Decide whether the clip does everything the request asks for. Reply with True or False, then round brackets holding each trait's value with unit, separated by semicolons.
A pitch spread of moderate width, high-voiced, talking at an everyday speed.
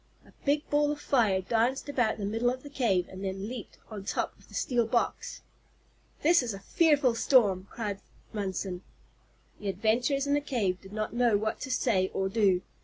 True (4.9 semitones; 225 Hz; 190 wpm)